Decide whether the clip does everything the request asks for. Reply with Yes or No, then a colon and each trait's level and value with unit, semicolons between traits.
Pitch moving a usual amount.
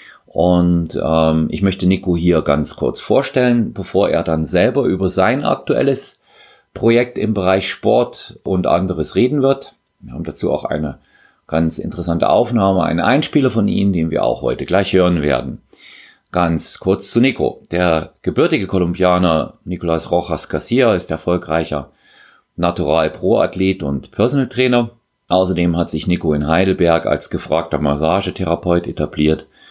Yes: average, 3.0 semitones